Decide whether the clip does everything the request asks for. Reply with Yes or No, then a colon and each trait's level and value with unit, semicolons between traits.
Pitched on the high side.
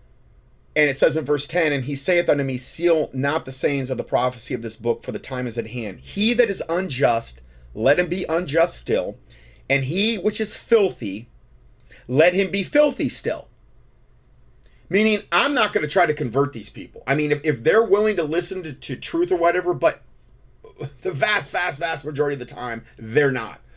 No: medium, 150 Hz